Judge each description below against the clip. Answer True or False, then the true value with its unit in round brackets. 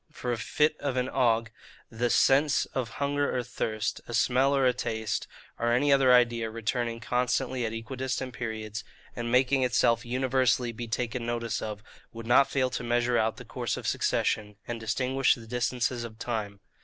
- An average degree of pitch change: False (2.1 semitones)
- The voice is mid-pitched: False (120 Hz)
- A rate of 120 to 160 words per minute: False (180 wpm)